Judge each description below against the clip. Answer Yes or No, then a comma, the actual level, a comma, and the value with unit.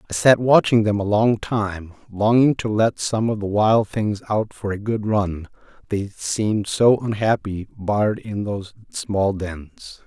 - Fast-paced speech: No, average, 175 wpm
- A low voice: Yes, low, 105 Hz